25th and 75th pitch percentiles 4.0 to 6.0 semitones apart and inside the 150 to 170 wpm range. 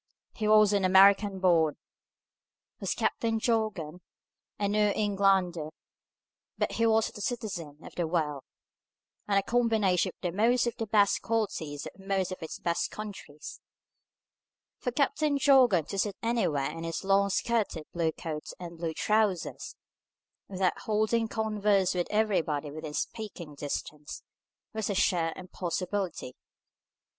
No: average, 4.4 semitones; slow, 135 wpm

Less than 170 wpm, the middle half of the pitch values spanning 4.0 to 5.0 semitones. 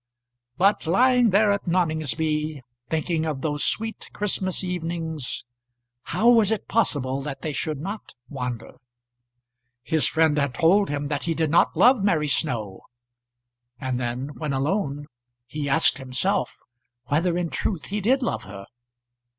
No: average, 140 wpm; wide, 5.4 semitones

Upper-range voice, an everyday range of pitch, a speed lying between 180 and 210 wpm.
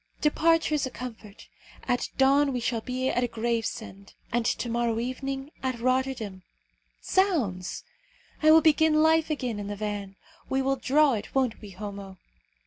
No: very high, 250 Hz; average, 4.2 semitones; average, 155 wpm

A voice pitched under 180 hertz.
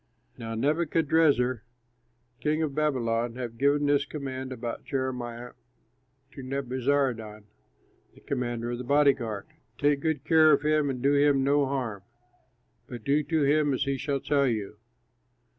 Yes: low, 135 Hz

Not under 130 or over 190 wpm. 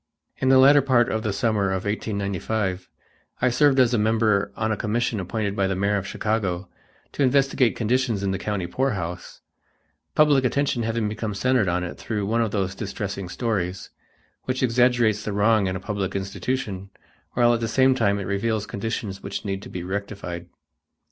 Yes: average, 180 wpm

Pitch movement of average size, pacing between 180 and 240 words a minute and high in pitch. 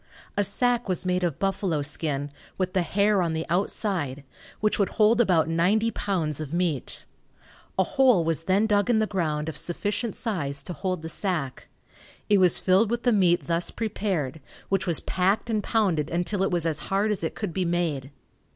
No: average, 4.2 semitones; average, 190 wpm; medium, 180 Hz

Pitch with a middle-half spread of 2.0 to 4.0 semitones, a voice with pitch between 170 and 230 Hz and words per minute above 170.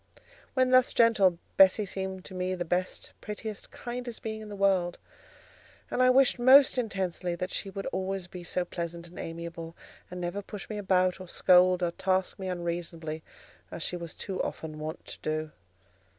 Yes: average, 2.9 semitones; medium, 185 Hz; average, 180 wpm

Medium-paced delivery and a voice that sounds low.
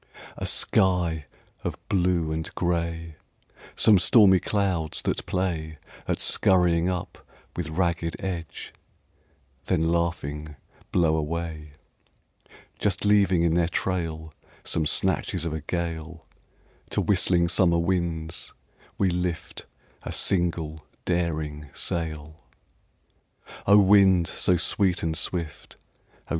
No: slow, 110 wpm; very low, 85 Hz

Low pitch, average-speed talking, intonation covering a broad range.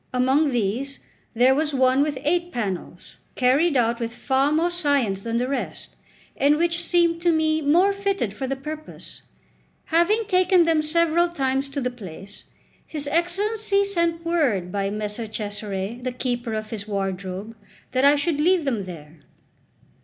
No: very high, 275 Hz; average, 160 wpm; wide, 6.9 semitones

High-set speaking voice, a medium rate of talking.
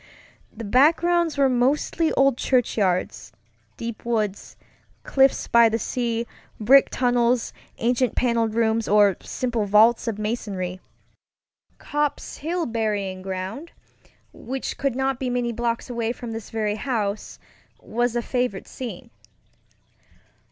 No: high, 235 Hz; slow, 120 wpm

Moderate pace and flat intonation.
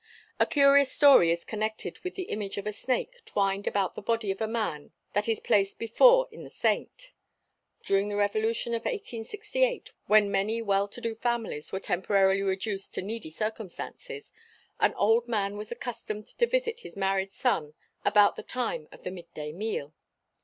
No: average, 175 wpm; average, 3.7 semitones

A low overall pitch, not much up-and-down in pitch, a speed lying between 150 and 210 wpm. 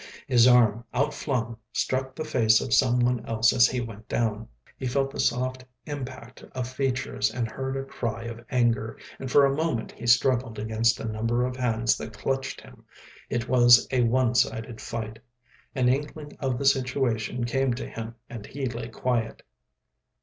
Yes: low, 120 Hz; narrow, 2.3 semitones; average, 170 wpm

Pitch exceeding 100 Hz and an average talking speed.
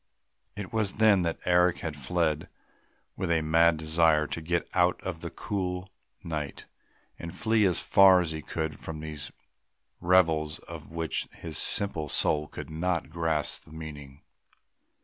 No: very low, 80 Hz; average, 155 wpm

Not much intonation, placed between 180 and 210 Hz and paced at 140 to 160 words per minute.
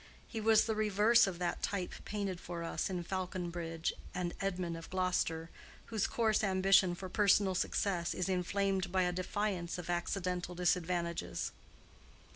Yes: narrow, 2.2 semitones; medium, 185 Hz; average, 145 wpm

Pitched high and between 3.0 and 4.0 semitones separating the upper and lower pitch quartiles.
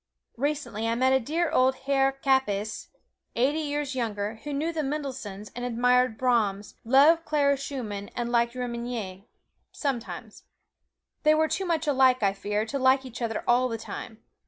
Yes: very high, 255 Hz; average, 3.7 semitones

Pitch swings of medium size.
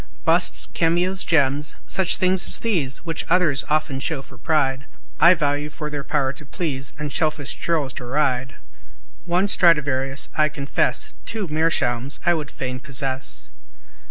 Yes: average, 3.6 semitones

